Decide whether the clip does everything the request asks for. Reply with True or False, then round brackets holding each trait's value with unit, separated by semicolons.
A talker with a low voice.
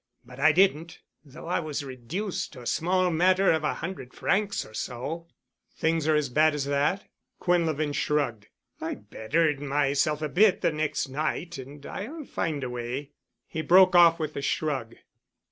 False (155 Hz)